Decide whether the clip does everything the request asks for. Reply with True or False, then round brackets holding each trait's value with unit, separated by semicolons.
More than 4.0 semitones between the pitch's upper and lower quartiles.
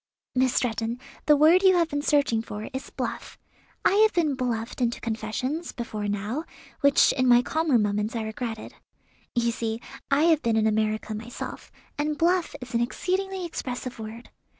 True (5.4 semitones)